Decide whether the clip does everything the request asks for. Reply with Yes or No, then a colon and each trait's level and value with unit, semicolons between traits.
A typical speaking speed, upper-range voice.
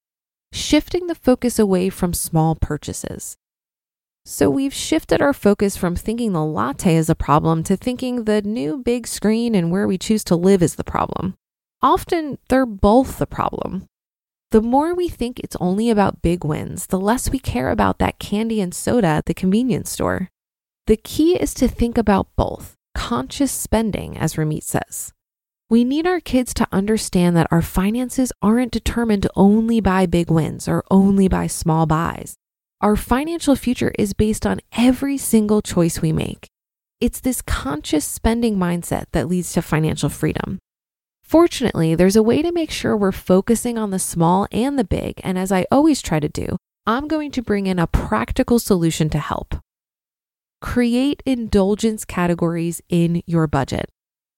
Yes: average, 170 wpm; high, 205 Hz